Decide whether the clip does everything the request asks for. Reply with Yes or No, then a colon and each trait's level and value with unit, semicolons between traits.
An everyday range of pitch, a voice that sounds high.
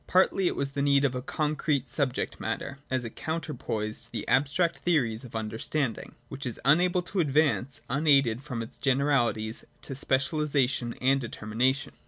No: average, 3.5 semitones; low, 135 Hz